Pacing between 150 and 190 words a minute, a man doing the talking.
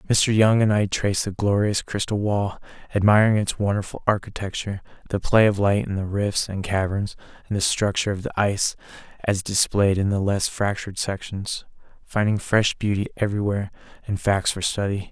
Yes: average, 170 wpm; male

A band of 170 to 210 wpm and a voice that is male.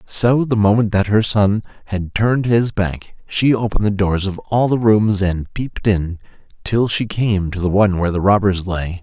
Yes: fast, 205 wpm; male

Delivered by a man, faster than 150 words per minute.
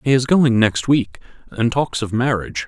Yes: male; average, 200 wpm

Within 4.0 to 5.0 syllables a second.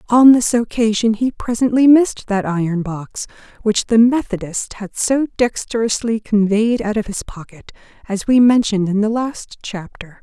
Yes: 4.7 syllables/s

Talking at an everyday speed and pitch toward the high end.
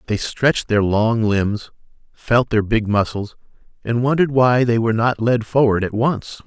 No: average, 175 wpm; low, 115 Hz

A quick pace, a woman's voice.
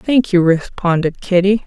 No: average, 145 wpm; female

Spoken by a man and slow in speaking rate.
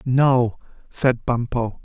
Yes: male; slow, 100 wpm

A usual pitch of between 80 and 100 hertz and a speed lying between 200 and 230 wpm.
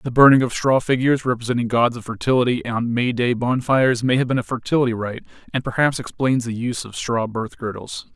No: low, 120 Hz; fast, 205 wpm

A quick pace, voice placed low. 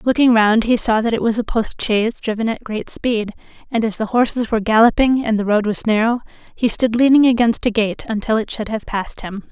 No: fast, 235 wpm; high, 225 Hz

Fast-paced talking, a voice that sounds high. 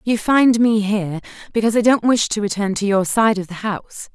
Yes: fast, 230 wpm; high, 210 Hz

